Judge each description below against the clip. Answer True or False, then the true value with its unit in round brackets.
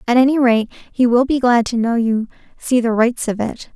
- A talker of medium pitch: False (240 Hz)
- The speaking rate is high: True (240 wpm)